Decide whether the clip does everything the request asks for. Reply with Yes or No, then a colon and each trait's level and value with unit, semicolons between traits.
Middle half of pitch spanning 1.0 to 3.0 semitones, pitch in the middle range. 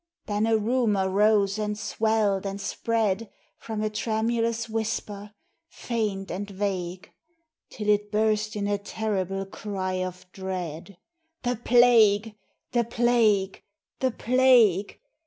No: narrow, 2.4 semitones; high, 210 Hz